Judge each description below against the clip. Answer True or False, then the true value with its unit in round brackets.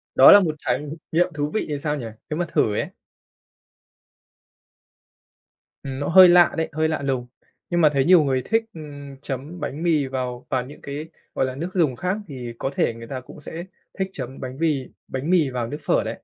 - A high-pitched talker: False (145 Hz)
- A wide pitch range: False (3.9 semitones)